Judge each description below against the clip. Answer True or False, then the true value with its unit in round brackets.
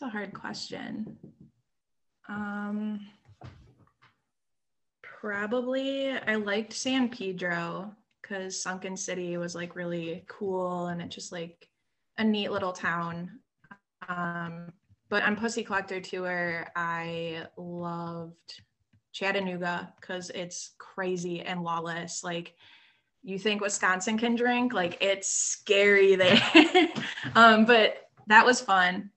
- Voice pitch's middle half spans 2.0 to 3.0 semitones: False (3.4 semitones)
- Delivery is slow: True (110 wpm)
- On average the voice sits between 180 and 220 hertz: True (190 Hz)